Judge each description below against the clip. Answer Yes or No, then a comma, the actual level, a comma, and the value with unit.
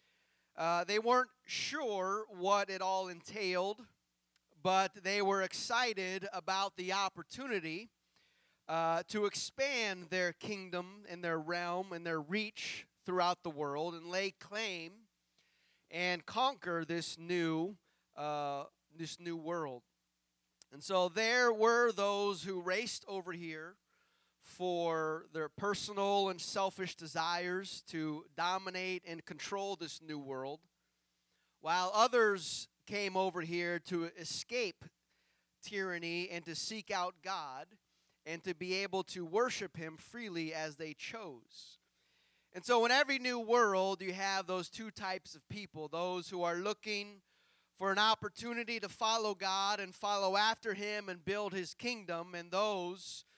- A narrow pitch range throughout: No, average, 3.5 semitones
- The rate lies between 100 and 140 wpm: Yes, slow, 135 wpm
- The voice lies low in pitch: No, medium, 185 Hz